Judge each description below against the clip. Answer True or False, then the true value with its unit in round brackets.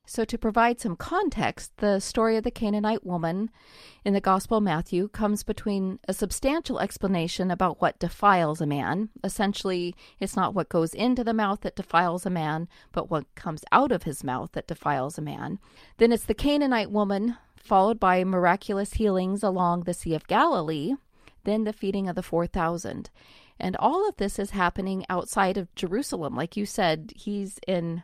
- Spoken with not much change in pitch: False (3.5 semitones)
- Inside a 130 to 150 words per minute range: False (180 wpm)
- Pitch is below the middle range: False (195 Hz)